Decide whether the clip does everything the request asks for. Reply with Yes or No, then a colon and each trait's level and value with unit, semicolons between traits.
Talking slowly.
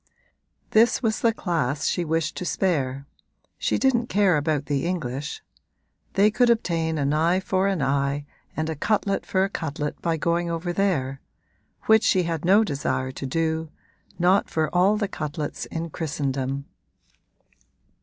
No: average, 155 wpm